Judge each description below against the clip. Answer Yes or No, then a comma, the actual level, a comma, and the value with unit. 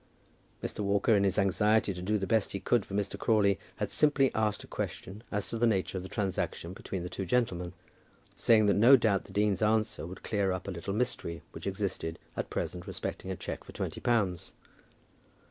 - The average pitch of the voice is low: Yes, low, 100 Hz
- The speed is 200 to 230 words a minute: Yes, fast, 205 wpm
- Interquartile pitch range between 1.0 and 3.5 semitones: Yes, narrow, 2.4 semitones